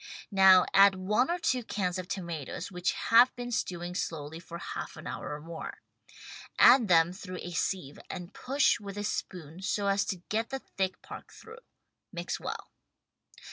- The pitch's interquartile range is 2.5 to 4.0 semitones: Yes, average, 3.6 semitones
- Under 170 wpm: No, average, 175 wpm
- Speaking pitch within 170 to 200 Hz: Yes, high, 190 Hz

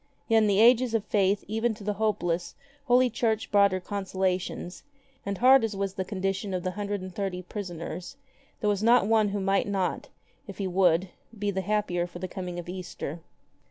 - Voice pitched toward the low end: No, high, 195 Hz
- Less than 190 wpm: No, average, 195 wpm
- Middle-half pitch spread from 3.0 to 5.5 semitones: No, narrow, 2.5 semitones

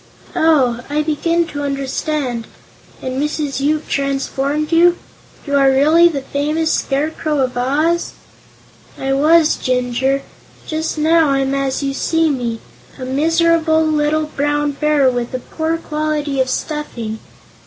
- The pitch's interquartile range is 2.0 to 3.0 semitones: Yes, narrow, 2.6 semitones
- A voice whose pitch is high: Yes, very high, 290 Hz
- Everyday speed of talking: No, slow, 130 wpm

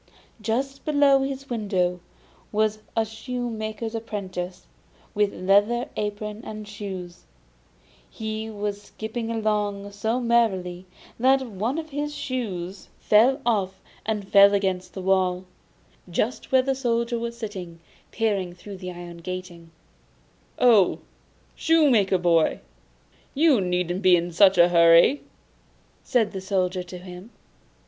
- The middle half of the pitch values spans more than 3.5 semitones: Yes, average, 4.2 semitones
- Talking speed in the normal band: No, slow, 125 wpm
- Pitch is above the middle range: Yes, high, 210 Hz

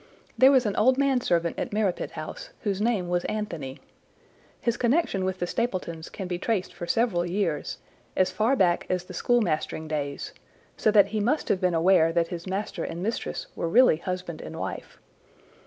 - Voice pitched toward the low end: No, medium, 185 Hz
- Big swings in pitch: No, average, 4.4 semitones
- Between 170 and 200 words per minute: Yes, average, 185 wpm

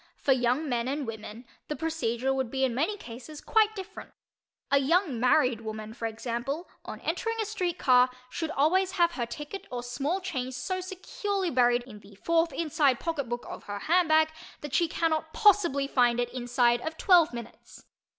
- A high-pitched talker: Yes, very high, 275 Hz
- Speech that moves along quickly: No, average, 180 wpm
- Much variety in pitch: Yes, wide, 5.8 semitones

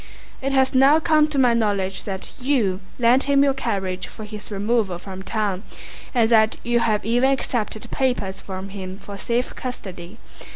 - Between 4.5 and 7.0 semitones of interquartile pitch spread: Yes, average, 5.0 semitones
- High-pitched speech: Yes, high, 220 Hz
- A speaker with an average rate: Yes, average, 170 wpm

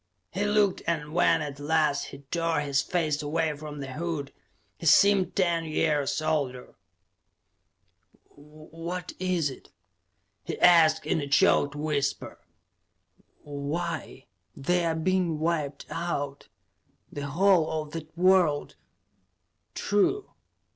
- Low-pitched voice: No, medium, 155 Hz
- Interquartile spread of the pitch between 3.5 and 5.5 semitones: No, average, 2.9 semitones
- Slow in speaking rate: Yes, slow, 115 wpm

